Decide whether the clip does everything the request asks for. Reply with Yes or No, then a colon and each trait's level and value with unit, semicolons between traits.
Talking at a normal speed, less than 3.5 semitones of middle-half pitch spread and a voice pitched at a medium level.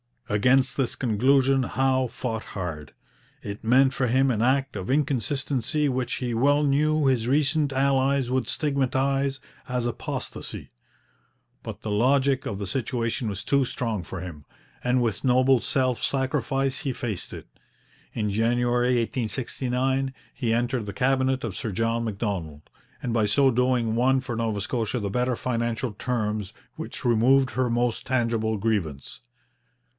No: average, 145 wpm; average, 3.0 semitones; low, 125 Hz